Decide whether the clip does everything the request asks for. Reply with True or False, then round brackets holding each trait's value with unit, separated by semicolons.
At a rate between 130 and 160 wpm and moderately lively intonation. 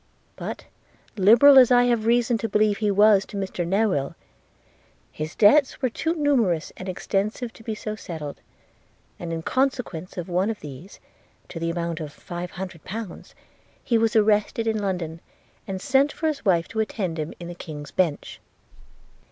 False (170 wpm; 4.9 semitones)